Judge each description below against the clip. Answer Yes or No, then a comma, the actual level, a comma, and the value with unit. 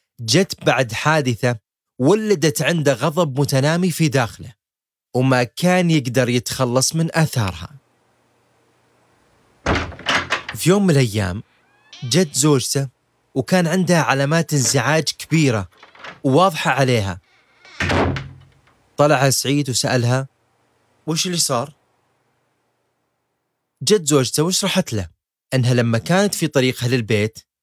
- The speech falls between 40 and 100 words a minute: Yes, average, 95 wpm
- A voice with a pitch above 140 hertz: No, low, 135 Hz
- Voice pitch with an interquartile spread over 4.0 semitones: Yes, average, 4.4 semitones